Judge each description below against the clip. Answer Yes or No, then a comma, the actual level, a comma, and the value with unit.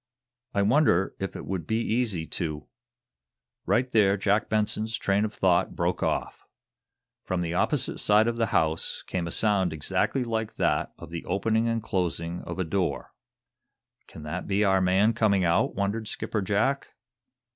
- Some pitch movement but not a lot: Yes, average, 3.9 semitones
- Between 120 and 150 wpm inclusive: No, average, 165 wpm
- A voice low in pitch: Yes, low, 100 Hz